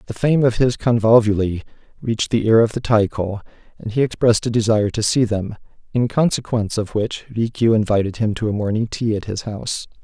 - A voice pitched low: Yes, low, 110 Hz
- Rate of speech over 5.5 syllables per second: Yes, 5.9 syllables/s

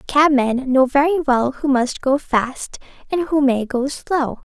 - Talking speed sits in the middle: Yes, average, 175 wpm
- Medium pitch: No, very high, 270 Hz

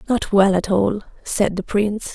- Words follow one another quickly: No, average, 195 wpm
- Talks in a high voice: Yes, high, 200 Hz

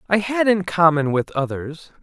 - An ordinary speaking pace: Yes, average, 180 wpm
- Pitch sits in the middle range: Yes, medium, 175 Hz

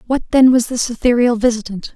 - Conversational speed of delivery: Yes, average, 185 wpm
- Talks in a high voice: Yes, high, 240 Hz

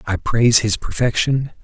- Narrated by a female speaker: No, male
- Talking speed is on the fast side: No, average, 145 wpm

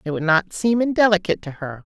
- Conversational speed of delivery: No, fast, 215 wpm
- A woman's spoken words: Yes, female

